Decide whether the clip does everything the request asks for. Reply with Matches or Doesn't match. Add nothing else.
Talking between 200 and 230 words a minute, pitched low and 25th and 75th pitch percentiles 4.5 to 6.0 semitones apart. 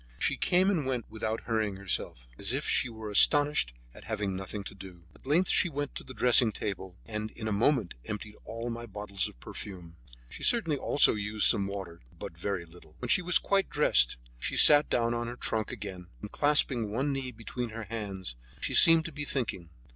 Matches